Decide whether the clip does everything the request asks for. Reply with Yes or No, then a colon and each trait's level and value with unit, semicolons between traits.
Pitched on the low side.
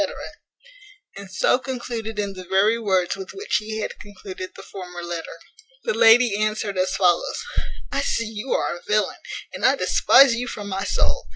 No: high, 205 Hz